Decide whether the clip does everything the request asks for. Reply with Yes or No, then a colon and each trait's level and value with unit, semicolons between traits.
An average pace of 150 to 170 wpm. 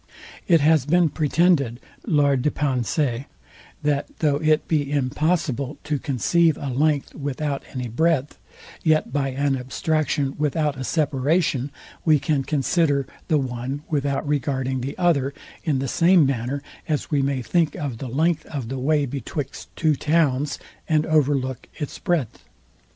No: average, 140 wpm